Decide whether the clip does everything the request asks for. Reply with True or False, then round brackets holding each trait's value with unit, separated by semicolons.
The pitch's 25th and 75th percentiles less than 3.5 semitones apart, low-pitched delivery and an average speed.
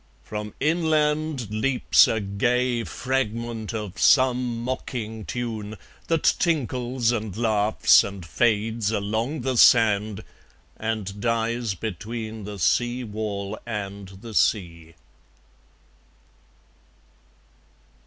False (2.9 semitones; 110 Hz; 90 wpm)